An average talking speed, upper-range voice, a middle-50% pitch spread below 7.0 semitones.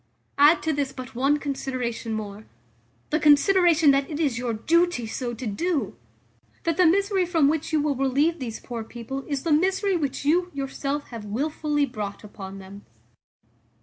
Yes: average, 170 wpm; very high, 280 Hz; average, 5.1 semitones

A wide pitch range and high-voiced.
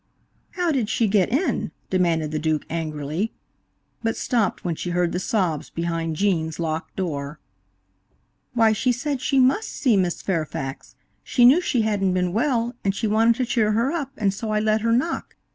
Yes: wide, 6.1 semitones; high, 205 Hz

